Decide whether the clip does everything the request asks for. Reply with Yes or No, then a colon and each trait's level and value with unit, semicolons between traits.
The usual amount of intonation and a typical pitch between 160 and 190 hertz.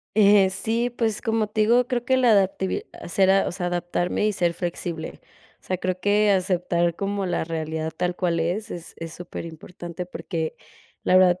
Yes: average, 3.2 semitones; medium, 185 Hz